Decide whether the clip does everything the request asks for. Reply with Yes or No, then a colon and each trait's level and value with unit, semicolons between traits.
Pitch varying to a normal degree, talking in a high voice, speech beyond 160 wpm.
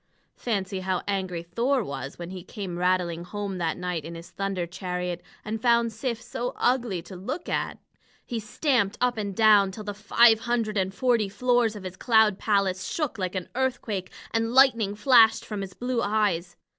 Yes: average, 4.0 semitones; high, 205 Hz; average, 180 wpm